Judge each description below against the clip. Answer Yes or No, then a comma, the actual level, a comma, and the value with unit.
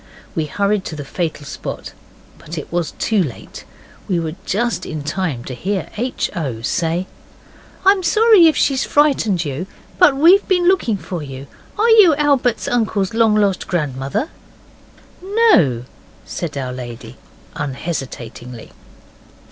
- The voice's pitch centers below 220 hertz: Yes, medium, 185 Hz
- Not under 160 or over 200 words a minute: No, average, 140 wpm